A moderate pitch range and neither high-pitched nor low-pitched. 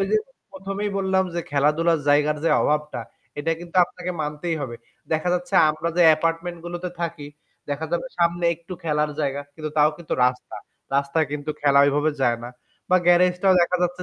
Yes: average, 3.0 semitones; medium, 165 Hz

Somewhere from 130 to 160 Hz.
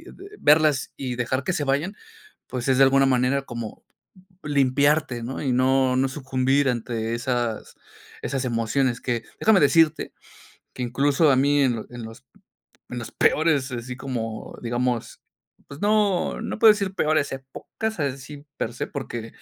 Yes: low, 135 Hz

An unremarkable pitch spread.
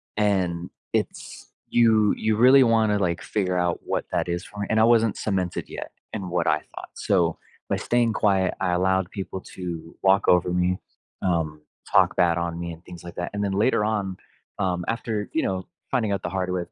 Yes: average, 3.2 semitones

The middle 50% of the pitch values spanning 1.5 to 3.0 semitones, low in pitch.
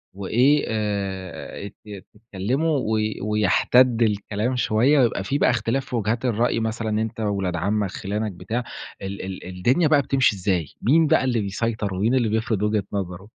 No: average, 3.5 semitones; low, 110 Hz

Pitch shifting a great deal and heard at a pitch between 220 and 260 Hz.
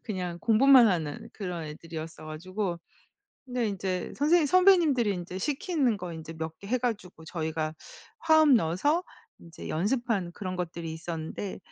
No: wide, 7.1 semitones; medium, 185 Hz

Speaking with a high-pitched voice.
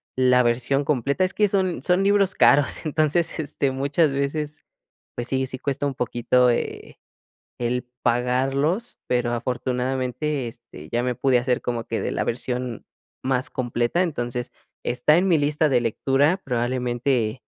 No: low, 130 Hz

